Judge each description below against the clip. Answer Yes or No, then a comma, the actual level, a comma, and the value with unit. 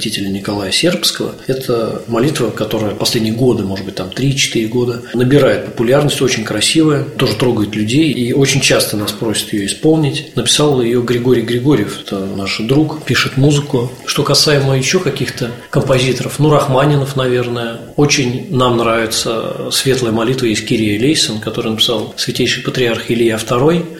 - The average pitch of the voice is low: Yes, low, 125 Hz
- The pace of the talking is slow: No, average, 145 wpm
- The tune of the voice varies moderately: Yes, average, 3.5 semitones